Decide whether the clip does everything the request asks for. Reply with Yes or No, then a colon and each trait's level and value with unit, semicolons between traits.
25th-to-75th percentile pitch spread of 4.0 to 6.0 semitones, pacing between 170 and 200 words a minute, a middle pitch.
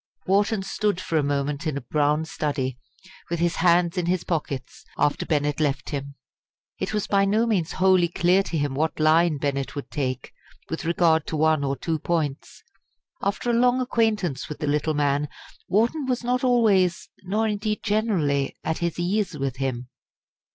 Yes: wide, 5.4 semitones; average, 175 wpm; medium, 165 Hz